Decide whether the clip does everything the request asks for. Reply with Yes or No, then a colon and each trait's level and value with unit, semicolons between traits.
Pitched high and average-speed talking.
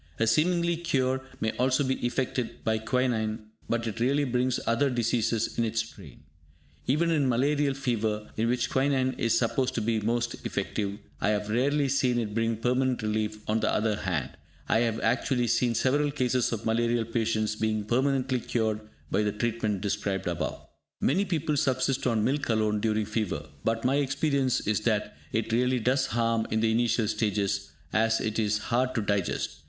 No: low, 115 Hz; average, 175 wpm